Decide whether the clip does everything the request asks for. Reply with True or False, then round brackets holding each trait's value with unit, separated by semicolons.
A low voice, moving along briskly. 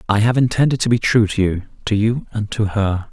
True (110 Hz; 230 wpm)